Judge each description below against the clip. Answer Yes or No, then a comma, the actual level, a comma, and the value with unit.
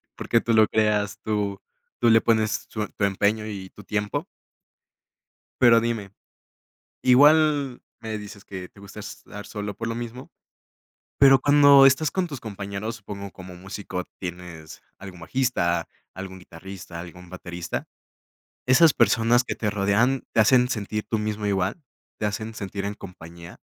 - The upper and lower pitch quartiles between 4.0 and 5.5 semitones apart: No, average, 3.3 semitones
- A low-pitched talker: Yes, low, 105 Hz